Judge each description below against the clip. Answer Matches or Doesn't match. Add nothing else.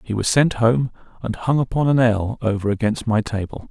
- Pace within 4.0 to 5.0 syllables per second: Doesn't match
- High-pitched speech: Doesn't match